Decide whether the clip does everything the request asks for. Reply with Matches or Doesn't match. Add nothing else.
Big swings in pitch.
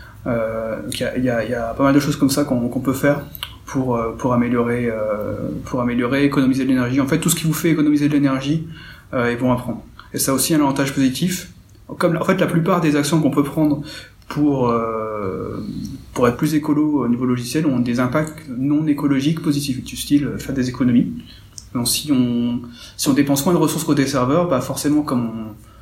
Doesn't match